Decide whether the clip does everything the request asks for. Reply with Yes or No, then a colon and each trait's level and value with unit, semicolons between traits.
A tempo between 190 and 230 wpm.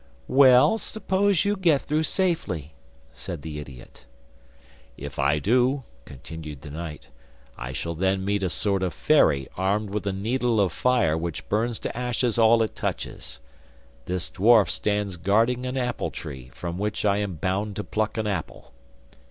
No: average, 160 wpm